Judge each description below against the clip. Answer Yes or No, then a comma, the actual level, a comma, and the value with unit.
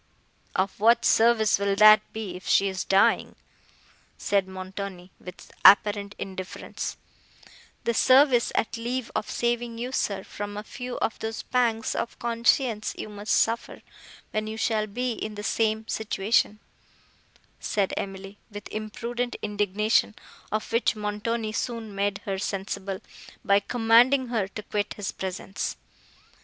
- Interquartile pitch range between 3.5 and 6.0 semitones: No, narrow, 2.6 semitones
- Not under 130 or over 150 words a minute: Yes, average, 140 wpm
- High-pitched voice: Yes, high, 215 Hz